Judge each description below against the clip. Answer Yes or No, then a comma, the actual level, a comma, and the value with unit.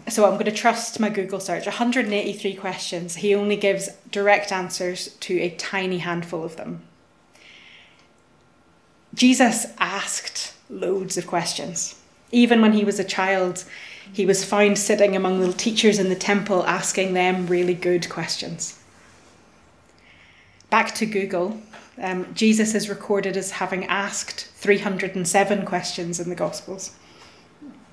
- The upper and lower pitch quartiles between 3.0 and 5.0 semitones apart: No, narrow, 2.5 semitones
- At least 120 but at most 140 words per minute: Yes, slow, 135 wpm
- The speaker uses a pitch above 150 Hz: Yes, high, 190 Hz